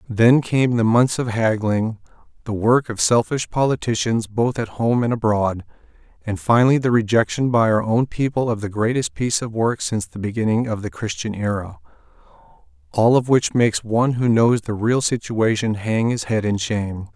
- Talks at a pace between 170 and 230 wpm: Yes, average, 180 wpm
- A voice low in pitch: Yes, low, 115 Hz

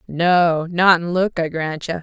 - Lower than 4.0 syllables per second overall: Yes, 3.8 syllables/s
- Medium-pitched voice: Yes, medium, 170 Hz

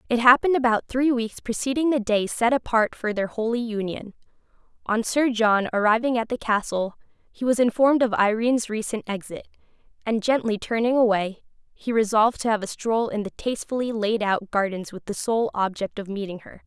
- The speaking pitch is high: Yes, high, 225 Hz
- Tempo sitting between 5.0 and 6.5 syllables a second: Yes, 5.5 syllables/s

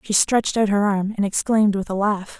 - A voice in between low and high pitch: No, high, 205 Hz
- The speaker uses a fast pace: Yes, fast, 250 wpm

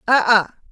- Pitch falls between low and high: No, high, 220 Hz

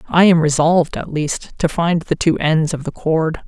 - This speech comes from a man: No, female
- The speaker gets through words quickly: Yes, fast, 225 wpm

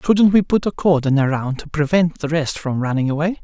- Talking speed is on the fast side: Yes, fast, 225 wpm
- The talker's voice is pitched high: No, medium, 160 Hz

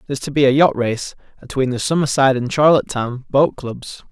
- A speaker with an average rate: Yes, average, 190 wpm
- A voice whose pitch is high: No, low, 135 Hz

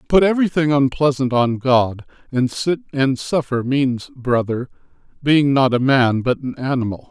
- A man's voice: Yes, male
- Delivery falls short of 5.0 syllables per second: Yes, 4.6 syllables/s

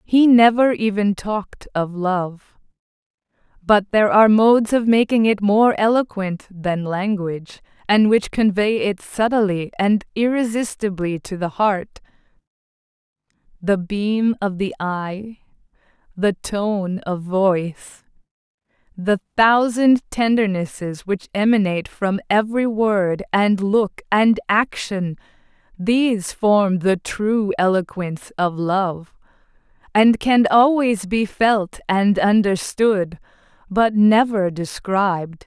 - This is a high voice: Yes, high, 205 Hz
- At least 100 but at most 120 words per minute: Yes, slow, 110 wpm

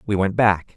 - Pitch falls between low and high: No, low, 100 Hz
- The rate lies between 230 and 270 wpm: Yes, fast, 235 wpm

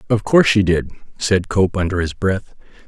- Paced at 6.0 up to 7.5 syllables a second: No, 5.2 syllables/s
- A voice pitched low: Yes, very low, 95 Hz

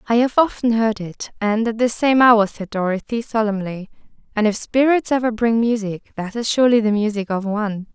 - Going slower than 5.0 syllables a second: No, 5.3 syllables/s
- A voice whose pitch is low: No, high, 220 Hz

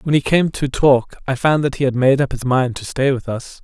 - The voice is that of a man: Yes, male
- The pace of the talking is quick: Yes, fast, 295 wpm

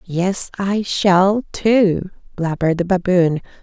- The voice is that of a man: No, female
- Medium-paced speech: No, slow, 115 wpm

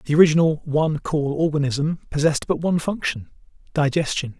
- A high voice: No, medium, 150 Hz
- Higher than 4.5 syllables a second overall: Yes, 6.0 syllables/s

